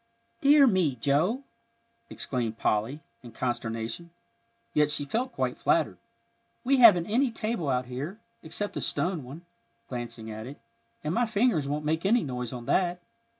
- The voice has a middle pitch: Yes, medium, 150 Hz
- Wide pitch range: Yes, wide, 8.8 semitones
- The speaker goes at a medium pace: Yes, average, 150 wpm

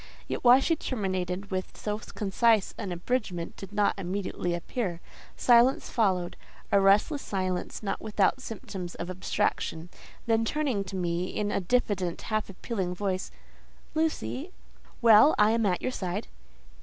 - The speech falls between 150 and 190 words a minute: No, slow, 135 wpm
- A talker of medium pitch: No, high, 200 Hz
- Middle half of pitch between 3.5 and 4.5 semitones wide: Yes, average, 3.9 semitones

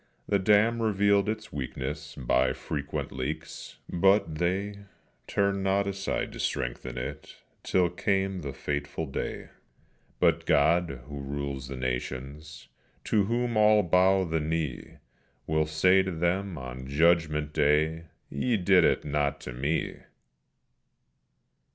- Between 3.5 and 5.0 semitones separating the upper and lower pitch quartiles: No, wide, 5.5 semitones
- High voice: No, very low, 80 Hz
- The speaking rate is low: Yes, slow, 125 wpm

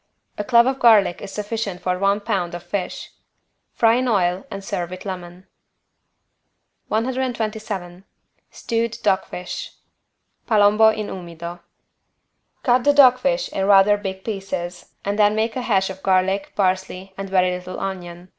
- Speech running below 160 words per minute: Yes, average, 145 wpm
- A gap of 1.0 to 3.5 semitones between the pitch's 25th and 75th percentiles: Yes, average, 3.1 semitones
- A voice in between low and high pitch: No, high, 195 Hz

